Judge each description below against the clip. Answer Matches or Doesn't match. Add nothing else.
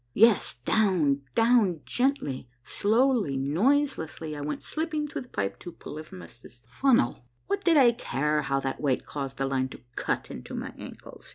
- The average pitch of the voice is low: Doesn't match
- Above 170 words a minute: Doesn't match